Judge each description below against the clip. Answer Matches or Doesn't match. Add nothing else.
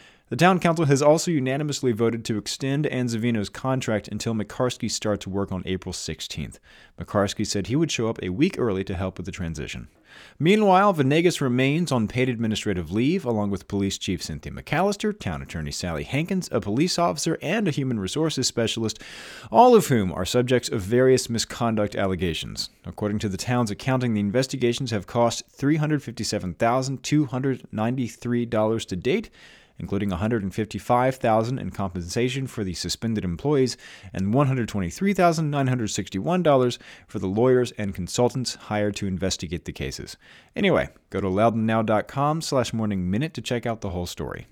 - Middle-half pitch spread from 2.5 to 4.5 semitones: Doesn't match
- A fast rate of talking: Doesn't match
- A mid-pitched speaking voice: Doesn't match